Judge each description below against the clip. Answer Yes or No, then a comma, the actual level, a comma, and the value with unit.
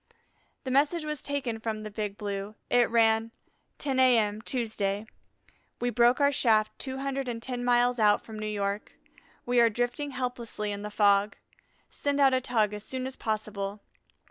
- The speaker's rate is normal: Yes, average, 170 wpm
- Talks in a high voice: Yes, high, 230 Hz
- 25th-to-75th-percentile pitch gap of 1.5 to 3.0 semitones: No, average, 3.5 semitones